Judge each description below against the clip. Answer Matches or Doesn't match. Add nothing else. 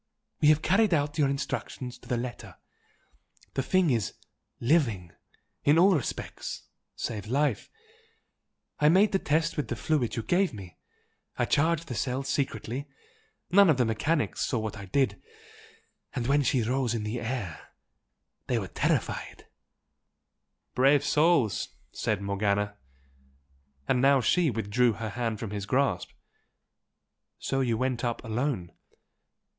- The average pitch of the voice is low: Matches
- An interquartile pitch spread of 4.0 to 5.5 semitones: Matches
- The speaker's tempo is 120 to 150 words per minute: Matches